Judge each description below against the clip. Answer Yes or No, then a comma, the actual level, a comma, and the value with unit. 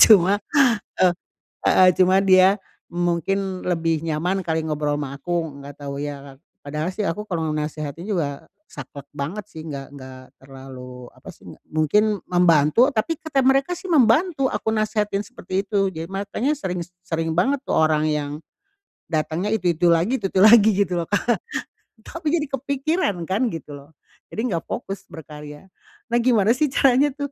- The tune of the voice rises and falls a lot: Yes, wide, 6.0 semitones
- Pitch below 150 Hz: No, medium, 180 Hz